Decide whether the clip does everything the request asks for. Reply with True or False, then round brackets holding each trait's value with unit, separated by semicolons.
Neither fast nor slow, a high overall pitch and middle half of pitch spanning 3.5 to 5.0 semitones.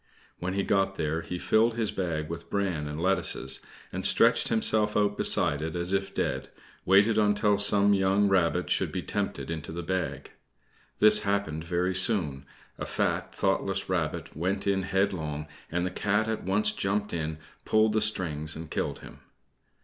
False (170 wpm; 95 Hz; 3.8 semitones)